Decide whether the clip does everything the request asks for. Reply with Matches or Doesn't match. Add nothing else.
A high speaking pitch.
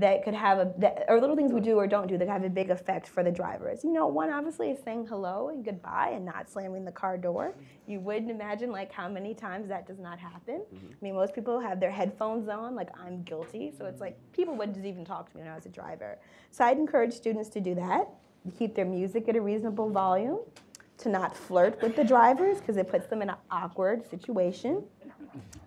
Matches